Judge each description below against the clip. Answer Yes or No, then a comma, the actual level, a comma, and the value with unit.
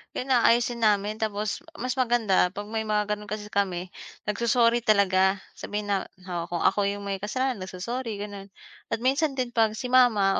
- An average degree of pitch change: Yes, average, 3.1 semitones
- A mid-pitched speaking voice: No, high, 210 Hz